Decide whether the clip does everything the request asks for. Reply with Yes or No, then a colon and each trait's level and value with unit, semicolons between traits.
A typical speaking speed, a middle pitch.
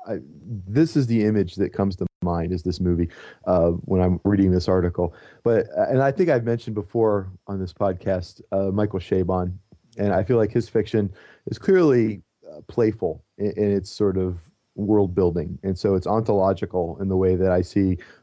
No: average, 190 wpm; very low, 95 Hz